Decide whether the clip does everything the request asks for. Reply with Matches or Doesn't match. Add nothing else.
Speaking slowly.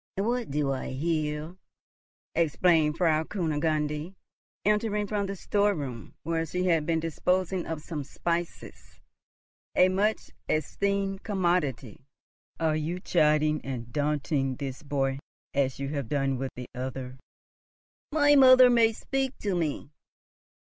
Matches